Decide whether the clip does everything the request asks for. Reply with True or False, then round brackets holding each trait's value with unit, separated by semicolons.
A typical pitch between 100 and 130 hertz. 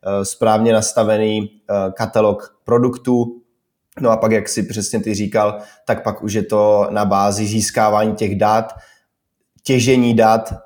True (110 Hz)